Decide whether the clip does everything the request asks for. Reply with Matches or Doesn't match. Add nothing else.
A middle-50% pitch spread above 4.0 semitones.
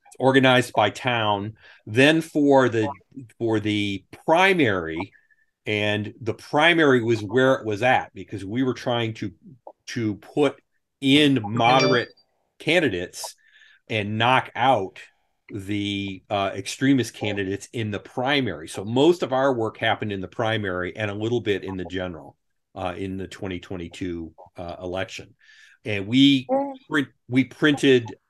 Matches